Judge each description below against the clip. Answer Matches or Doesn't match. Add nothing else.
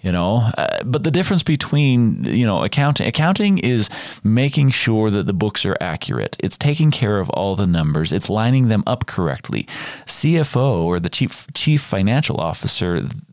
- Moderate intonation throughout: Doesn't match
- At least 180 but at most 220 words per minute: Doesn't match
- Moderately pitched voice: Doesn't match